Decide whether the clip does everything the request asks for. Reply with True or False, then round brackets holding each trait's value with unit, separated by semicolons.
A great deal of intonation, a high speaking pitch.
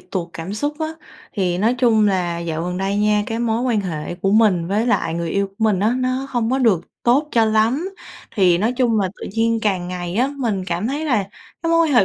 False (4.8 semitones; 215 Hz)